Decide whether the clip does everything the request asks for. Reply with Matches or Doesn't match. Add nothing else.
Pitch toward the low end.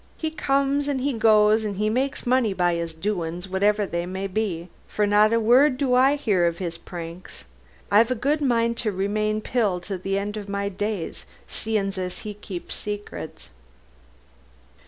Doesn't match